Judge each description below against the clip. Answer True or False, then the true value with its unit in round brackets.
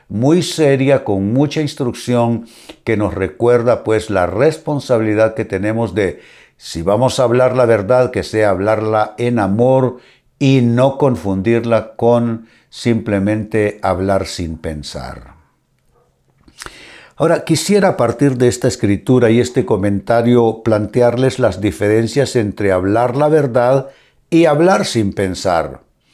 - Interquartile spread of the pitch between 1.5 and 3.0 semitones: False (3.7 semitones)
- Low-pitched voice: True (115 Hz)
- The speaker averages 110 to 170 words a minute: True (125 wpm)